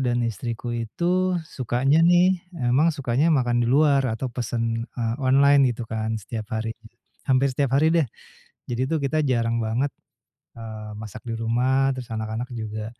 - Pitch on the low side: Yes, low, 120 Hz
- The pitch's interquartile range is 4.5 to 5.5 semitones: No, average, 3.4 semitones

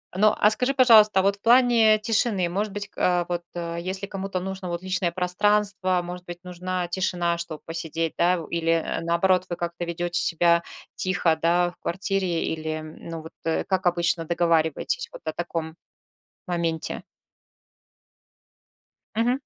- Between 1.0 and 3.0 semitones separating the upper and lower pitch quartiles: Yes, narrow, 2.5 semitones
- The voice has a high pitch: No, medium, 180 Hz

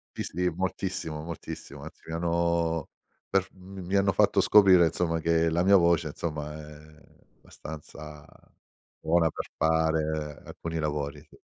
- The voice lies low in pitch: Yes, very low, 80 Hz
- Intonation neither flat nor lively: No, narrow, 2.1 semitones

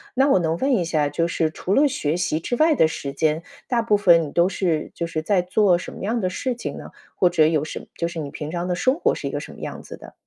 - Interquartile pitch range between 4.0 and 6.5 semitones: Yes, average, 4.6 semitones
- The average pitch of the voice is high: No, medium, 175 Hz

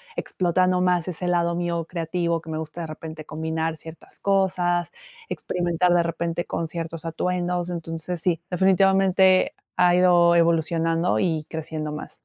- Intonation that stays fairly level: Yes, narrow, 1.7 semitones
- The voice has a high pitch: No, medium, 170 Hz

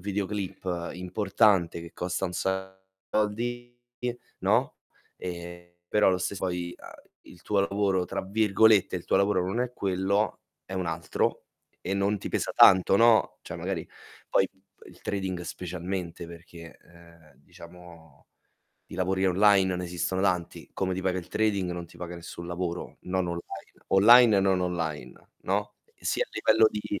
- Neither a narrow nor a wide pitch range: No, narrow, 2.3 semitones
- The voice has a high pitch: No, very low, 95 Hz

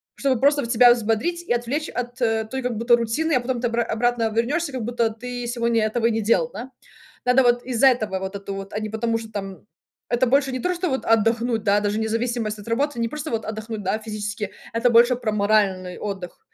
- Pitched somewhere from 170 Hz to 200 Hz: No, high, 230 Hz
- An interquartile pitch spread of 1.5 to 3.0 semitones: Yes, narrow, 2.5 semitones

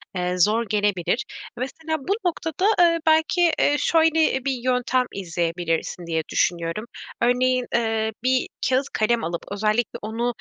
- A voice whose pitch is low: No, high, 240 Hz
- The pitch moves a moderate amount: No, wide, 6.3 semitones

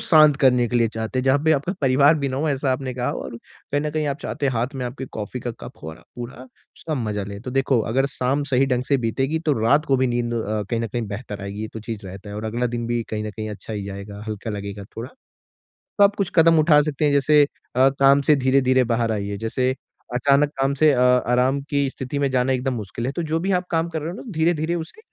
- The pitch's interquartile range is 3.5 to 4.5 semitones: Yes, average, 4.1 semitones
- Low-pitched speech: Yes, low, 130 Hz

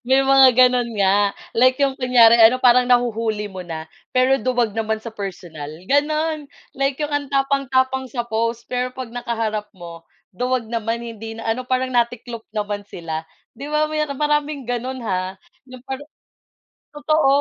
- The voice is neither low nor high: No, high, 245 Hz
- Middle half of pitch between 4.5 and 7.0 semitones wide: No, average, 3.3 semitones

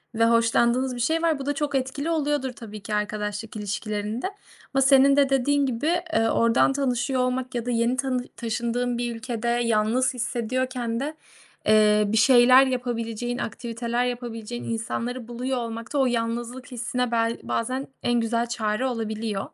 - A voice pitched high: Yes, high, 240 Hz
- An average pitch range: No, narrow, 2.2 semitones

